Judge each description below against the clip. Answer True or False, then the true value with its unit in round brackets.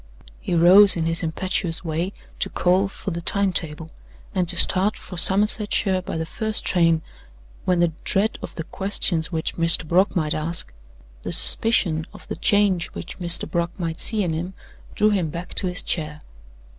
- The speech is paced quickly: False (180 wpm)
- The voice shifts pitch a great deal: False (2.8 semitones)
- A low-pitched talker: False (175 Hz)